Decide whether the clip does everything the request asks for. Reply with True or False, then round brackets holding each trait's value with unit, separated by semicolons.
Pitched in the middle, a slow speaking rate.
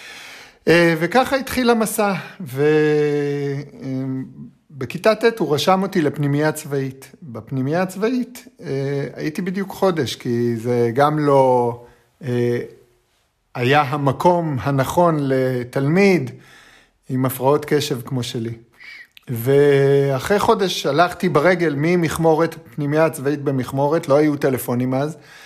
True (145 Hz; 95 wpm)